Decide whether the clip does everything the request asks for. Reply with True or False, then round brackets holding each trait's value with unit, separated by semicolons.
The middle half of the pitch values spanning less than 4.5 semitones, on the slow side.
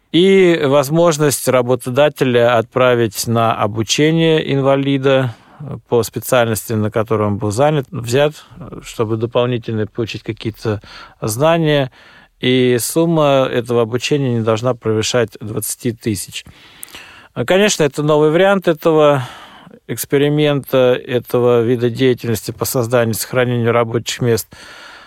True (4.0 semitones; 105 wpm)